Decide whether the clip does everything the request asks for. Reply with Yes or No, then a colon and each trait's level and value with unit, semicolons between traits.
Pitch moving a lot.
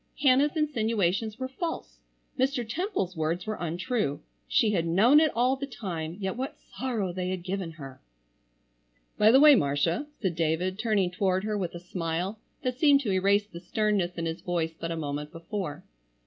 Yes: wide, 6.1 semitones